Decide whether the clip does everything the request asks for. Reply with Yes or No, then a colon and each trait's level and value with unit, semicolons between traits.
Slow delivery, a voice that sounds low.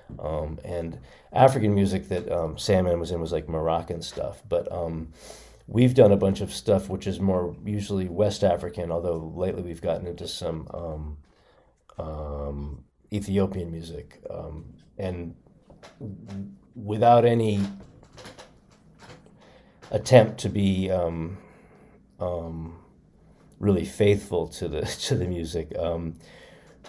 Yes: slow, 125 wpm; very low, 90 Hz